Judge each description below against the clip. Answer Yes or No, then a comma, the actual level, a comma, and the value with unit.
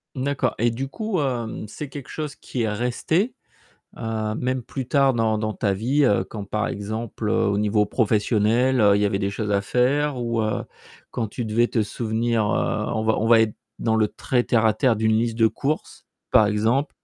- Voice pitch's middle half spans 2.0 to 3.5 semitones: Yes, average, 2.9 semitones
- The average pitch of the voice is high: No, low, 115 Hz